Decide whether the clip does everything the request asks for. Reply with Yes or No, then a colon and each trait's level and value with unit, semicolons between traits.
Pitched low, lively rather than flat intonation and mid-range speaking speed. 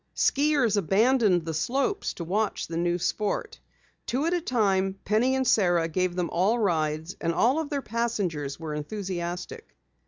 No: high, 195 Hz; wide, 6.1 semitones; average, 155 wpm